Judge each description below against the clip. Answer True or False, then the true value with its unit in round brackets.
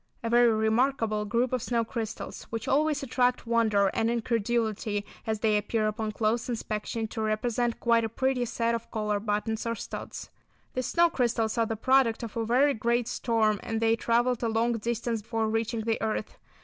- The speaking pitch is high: True (230 Hz)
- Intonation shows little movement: True (1.6 semitones)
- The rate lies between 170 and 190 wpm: True (185 wpm)